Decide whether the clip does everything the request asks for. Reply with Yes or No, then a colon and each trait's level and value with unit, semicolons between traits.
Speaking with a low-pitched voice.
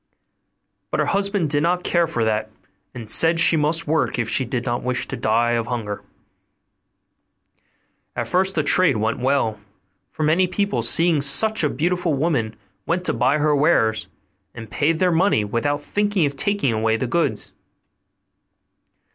No: medium, 145 Hz